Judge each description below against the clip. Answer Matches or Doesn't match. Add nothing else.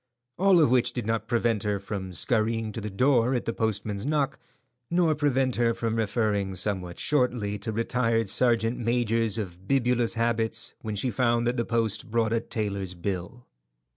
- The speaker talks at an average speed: Matches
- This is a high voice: Doesn't match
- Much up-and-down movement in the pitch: Doesn't match